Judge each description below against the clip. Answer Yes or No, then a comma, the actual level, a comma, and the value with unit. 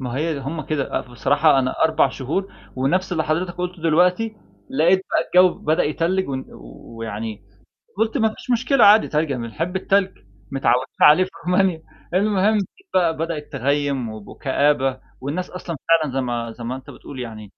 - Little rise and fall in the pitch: No, wide, 5.6 semitones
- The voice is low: No, medium, 155 Hz